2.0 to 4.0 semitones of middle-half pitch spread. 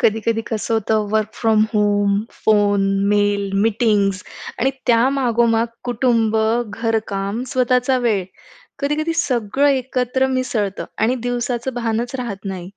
Yes: average, 3.2 semitones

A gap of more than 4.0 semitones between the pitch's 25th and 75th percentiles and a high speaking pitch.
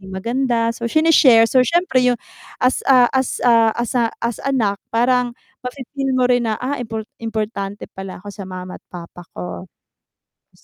No: average, 3.6 semitones; high, 235 Hz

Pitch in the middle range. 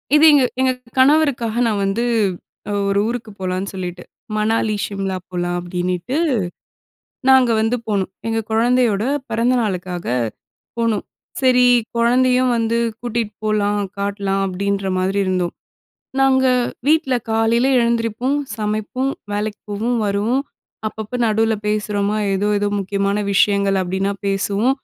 No: high, 215 Hz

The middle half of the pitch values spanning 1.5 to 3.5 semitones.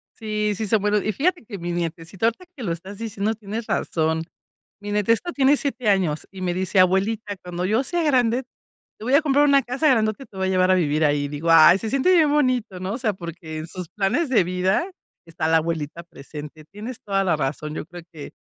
No: wide, 5.5 semitones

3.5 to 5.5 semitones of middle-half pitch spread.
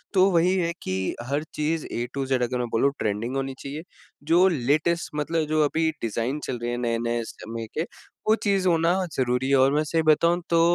Yes: average, 5.2 semitones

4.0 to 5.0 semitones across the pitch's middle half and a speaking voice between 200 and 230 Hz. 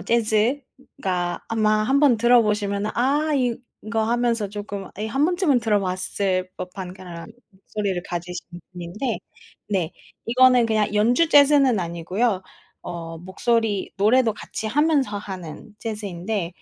Yes: average, 4.5 semitones; high, 215 Hz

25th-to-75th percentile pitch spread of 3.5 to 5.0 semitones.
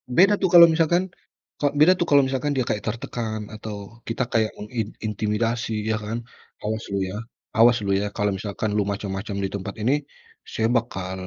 Yes: average, 3.8 semitones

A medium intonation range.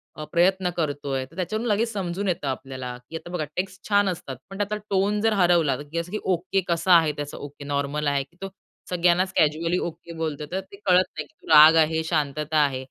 Yes: average, 4.2 semitones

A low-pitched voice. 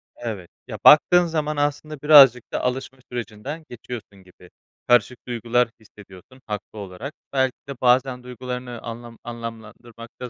Yes: low, 125 Hz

